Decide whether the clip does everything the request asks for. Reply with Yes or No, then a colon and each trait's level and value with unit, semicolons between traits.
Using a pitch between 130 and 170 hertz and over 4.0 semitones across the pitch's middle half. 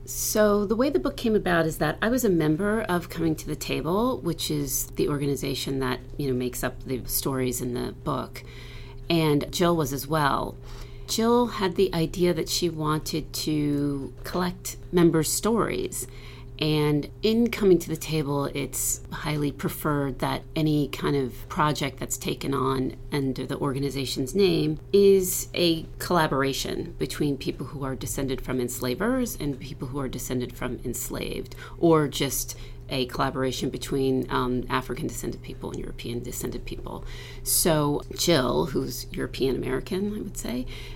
Yes: medium, 140 Hz; average, 4.5 semitones